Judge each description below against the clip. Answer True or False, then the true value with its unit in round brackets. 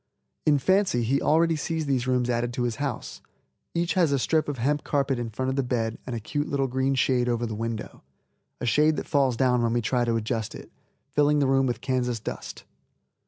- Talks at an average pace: False (220 wpm)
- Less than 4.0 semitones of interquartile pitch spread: True (3.3 semitones)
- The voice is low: True (130 Hz)